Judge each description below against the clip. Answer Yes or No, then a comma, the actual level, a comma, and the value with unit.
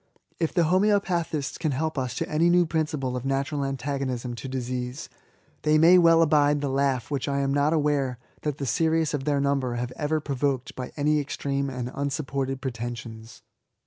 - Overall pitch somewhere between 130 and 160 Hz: Yes, medium, 140 Hz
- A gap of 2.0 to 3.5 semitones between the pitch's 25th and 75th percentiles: Yes, average, 2.9 semitones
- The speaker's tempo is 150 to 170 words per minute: No, average, 180 wpm